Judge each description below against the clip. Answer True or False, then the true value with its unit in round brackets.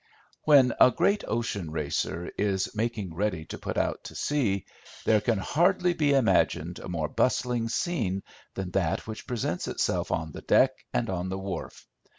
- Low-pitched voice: True (105 Hz)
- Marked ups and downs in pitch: True (5.7 semitones)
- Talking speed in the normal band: True (165 wpm)